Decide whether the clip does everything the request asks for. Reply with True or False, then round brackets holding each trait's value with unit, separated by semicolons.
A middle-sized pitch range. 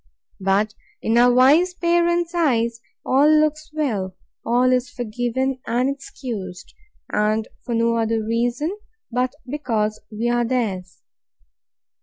True (3.9 semitones)